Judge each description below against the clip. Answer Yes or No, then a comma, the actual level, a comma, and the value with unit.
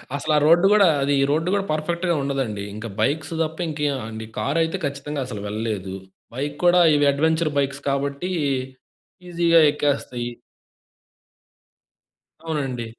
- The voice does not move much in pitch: No, average, 3.3 semitones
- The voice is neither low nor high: Yes, medium, 145 Hz